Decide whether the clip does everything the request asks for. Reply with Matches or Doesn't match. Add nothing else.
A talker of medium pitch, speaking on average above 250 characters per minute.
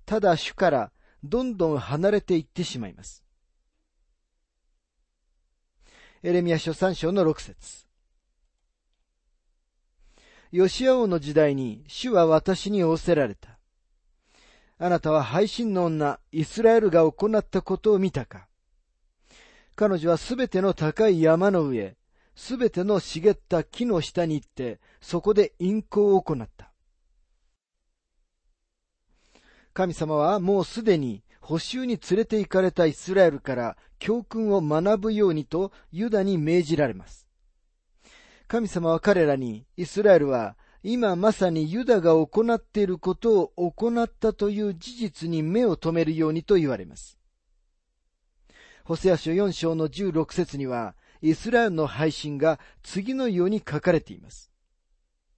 Doesn't match